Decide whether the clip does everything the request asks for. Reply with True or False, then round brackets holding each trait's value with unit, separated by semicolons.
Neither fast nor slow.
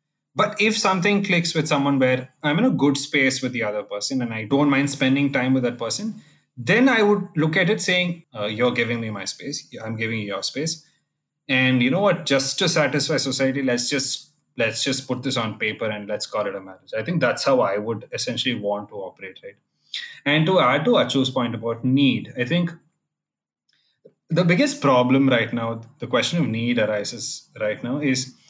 False (210 wpm)